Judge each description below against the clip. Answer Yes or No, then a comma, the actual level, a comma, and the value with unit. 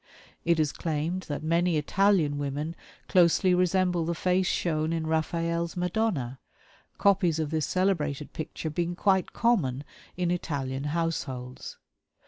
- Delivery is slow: Yes, slow, 125 wpm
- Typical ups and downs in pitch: Yes, average, 3.2 semitones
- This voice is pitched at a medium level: Yes, medium, 165 Hz